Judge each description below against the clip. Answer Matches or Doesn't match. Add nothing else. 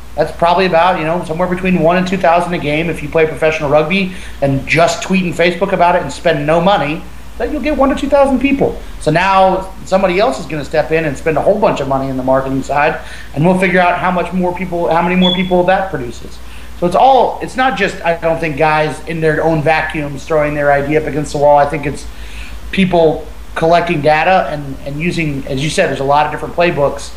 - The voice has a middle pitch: Matches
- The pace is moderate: Doesn't match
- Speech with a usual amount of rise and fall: Matches